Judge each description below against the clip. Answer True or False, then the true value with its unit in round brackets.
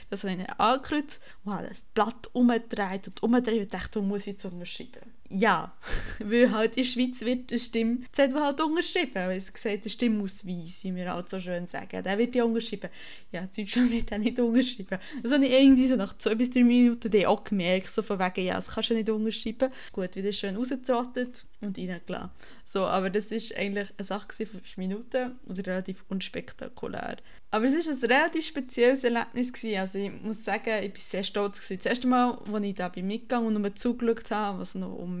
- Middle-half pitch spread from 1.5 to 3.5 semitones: False (4.0 semitones)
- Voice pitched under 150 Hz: False (220 Hz)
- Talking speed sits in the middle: False (215 wpm)